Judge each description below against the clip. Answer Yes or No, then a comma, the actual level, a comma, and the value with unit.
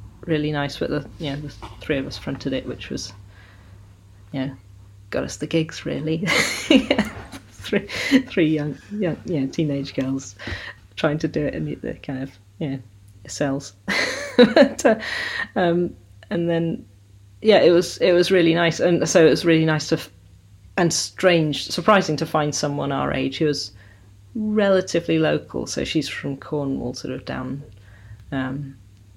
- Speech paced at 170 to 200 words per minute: No, average, 160 wpm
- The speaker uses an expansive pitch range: Yes, wide, 8.9 semitones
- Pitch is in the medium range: Yes, medium, 145 Hz